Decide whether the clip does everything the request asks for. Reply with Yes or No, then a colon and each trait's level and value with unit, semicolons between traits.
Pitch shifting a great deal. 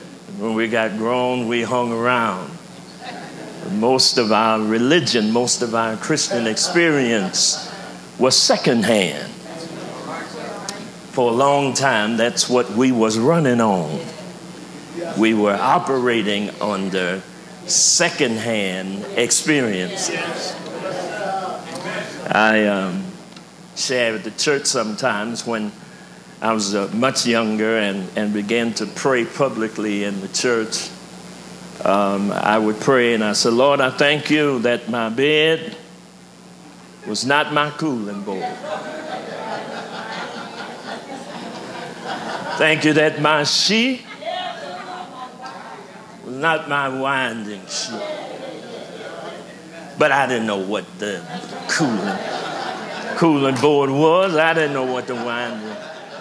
Yes: wide, 5.7 semitones